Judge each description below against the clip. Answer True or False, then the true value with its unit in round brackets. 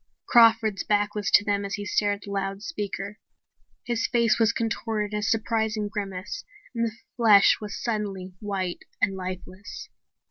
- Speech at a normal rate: True (155 wpm)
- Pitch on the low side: False (210 Hz)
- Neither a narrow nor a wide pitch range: False (2.1 semitones)